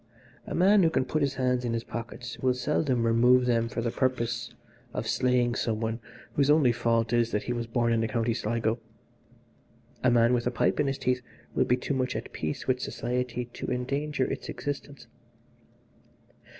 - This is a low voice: Yes, low, 125 Hz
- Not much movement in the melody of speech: Yes, narrow, 1.8 semitones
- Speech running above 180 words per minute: Yes, average, 190 wpm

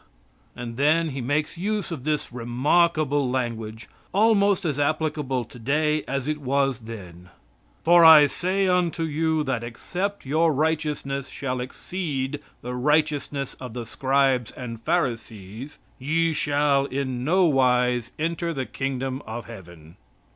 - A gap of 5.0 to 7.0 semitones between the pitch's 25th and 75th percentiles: No, average, 4.2 semitones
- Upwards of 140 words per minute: No, slow, 135 wpm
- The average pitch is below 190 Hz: Yes, medium, 140 Hz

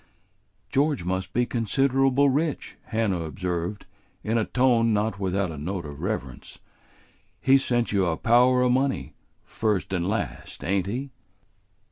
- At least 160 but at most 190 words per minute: No, average, 140 wpm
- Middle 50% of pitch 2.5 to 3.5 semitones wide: No, wide, 5.6 semitones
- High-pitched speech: No, low, 110 Hz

